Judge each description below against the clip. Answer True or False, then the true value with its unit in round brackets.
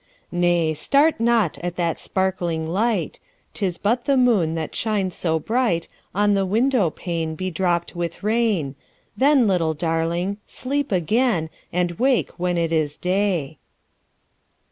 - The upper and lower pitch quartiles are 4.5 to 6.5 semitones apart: True (5.0 semitones)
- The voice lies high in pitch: False (180 Hz)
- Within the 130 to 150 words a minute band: True (140 wpm)